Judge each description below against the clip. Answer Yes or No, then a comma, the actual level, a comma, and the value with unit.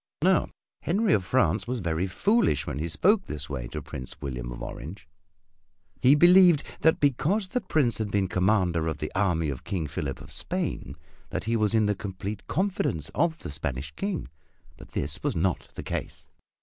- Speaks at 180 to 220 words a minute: Yes, average, 185 wpm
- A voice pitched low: Yes, low, 100 Hz